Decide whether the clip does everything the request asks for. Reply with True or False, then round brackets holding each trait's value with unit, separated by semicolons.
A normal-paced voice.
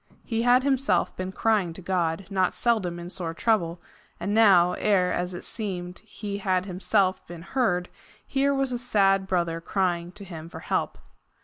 True (175 wpm)